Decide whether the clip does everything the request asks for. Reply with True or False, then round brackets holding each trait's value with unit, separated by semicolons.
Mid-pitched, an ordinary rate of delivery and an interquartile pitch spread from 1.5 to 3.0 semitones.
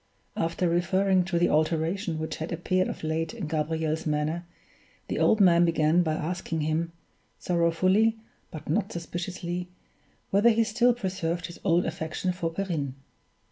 True (170 Hz; 145 wpm; 2.6 semitones)